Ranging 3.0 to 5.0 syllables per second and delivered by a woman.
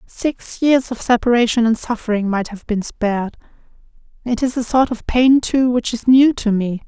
Yes: 4.8 syllables/s; female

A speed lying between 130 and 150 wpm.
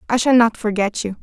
No: fast, 245 wpm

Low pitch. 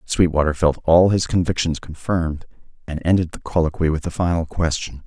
Yes: very low, 85 Hz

